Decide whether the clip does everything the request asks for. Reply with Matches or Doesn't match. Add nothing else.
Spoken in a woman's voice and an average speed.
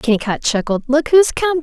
Matches